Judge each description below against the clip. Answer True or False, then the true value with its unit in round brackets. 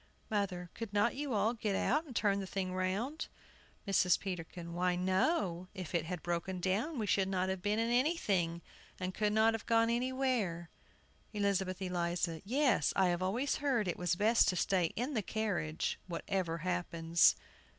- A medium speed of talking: True (170 wpm)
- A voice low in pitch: False (190 Hz)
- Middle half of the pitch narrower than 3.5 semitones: False (4.1 semitones)